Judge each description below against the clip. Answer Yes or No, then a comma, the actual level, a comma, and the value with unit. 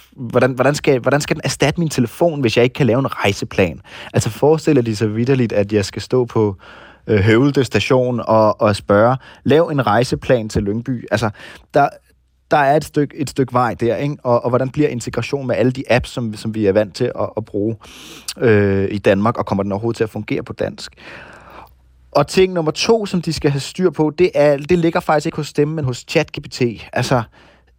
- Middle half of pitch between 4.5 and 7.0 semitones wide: Yes, average, 5.3 semitones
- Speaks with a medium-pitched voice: No, low, 125 Hz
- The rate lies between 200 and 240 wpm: Yes, average, 220 wpm